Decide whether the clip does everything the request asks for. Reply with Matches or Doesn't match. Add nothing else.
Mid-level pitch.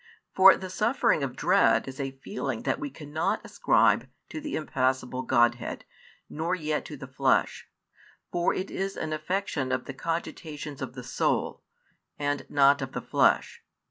Matches